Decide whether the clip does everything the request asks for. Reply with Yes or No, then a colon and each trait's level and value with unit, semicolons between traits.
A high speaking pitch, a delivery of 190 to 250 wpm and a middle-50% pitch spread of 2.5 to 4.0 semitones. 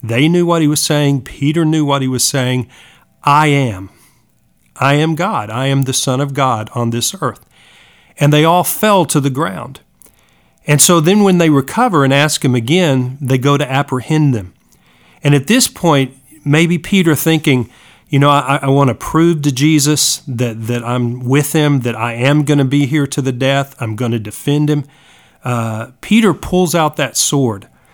No: medium, 140 Hz; average, 195 wpm; average, 3.4 semitones